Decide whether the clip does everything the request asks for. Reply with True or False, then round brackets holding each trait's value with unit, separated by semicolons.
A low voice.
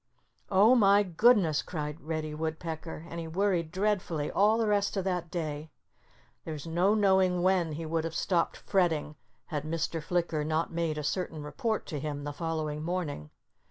False (165 Hz)